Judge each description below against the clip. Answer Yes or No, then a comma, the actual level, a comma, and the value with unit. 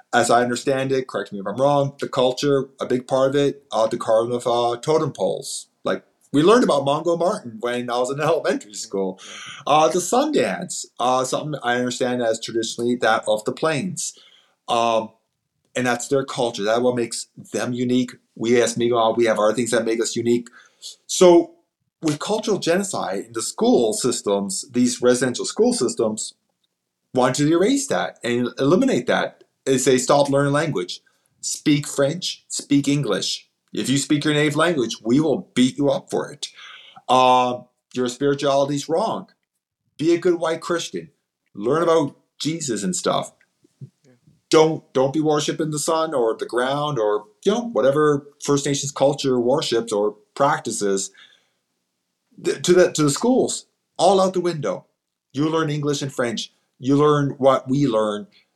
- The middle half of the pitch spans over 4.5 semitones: No, average, 4.0 semitones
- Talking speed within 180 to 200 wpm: No, average, 165 wpm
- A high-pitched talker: No, low, 135 Hz